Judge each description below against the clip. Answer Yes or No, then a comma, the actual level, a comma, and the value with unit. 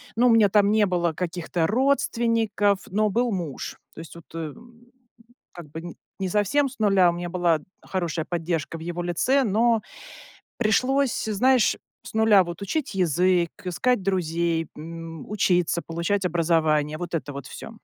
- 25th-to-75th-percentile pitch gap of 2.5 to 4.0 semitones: No, average, 4.6 semitones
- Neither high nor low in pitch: Yes, medium, 180 Hz